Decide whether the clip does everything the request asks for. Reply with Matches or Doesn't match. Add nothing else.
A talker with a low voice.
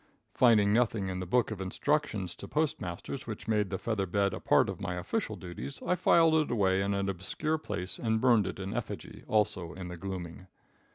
Matches